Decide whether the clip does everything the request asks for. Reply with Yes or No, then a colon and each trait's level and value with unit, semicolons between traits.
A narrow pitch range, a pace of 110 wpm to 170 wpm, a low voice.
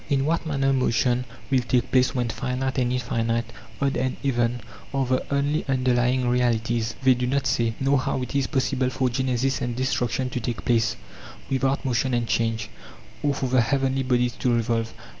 No: narrow, 1.9 semitones; average, 180 wpm; low, 125 Hz